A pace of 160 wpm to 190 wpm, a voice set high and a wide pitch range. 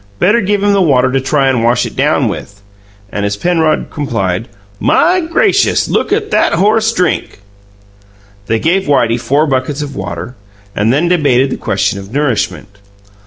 No: average, 165 wpm; low, 135 Hz; wide, 7.9 semitones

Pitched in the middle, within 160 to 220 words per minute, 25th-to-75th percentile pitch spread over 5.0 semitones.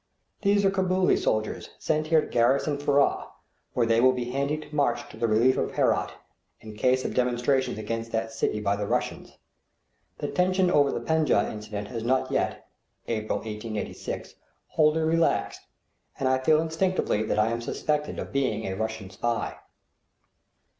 No: low, 130 Hz; average, 165 wpm; wide, 5.6 semitones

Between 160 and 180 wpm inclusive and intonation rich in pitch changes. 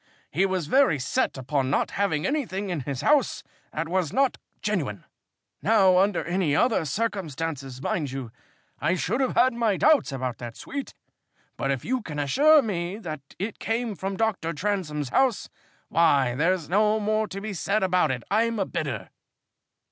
Yes: average, 170 wpm; wide, 6.8 semitones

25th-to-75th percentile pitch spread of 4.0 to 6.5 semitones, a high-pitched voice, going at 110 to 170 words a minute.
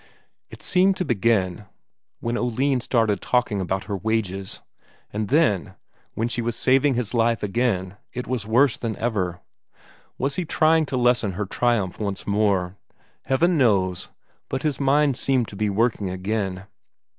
No: average, 4.5 semitones; low, 115 Hz; average, 155 wpm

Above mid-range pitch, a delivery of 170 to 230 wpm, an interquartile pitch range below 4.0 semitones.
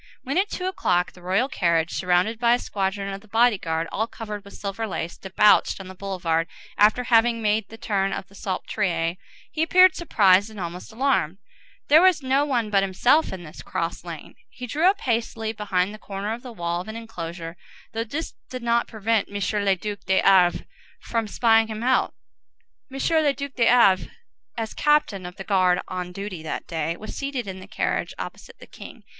No: high, 210 Hz; average, 200 wpm; average, 4.3 semitones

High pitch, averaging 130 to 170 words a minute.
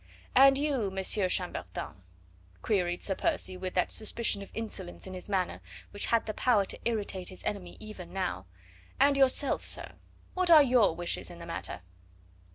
Yes: high, 200 Hz; average, 165 wpm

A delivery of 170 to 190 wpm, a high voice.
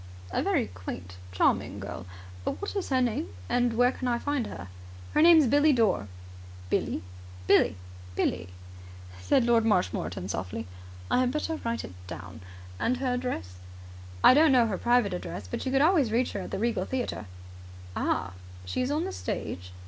Yes: average, 175 wpm; high, 235 Hz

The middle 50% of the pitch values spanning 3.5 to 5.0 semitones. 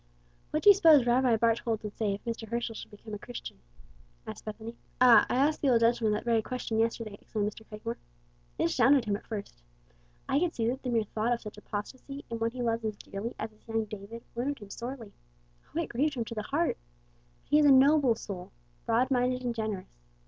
No: average, 3.0 semitones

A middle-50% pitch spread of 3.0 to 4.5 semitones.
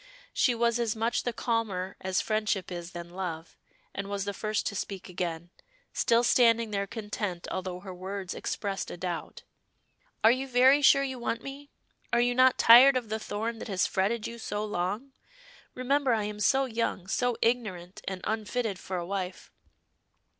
Yes: average, 4.2 semitones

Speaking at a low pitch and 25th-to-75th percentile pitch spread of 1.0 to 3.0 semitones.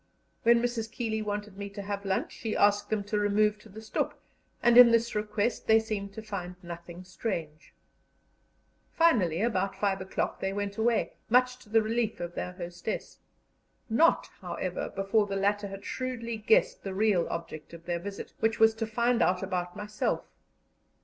No: high, 210 Hz; narrow, 2.6 semitones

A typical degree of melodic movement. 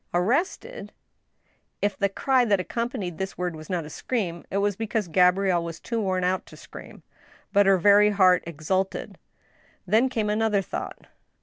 Yes: average, 3.4 semitones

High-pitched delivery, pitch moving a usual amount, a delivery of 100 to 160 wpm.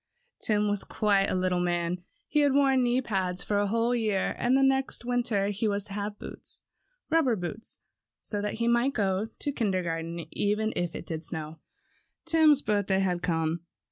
No: high, 205 Hz; average, 4.7 semitones; average, 175 wpm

